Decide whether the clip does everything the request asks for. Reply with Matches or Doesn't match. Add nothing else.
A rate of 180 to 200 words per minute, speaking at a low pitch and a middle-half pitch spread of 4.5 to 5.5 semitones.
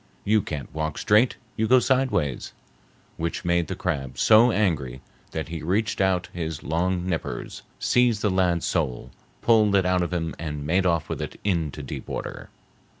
Doesn't match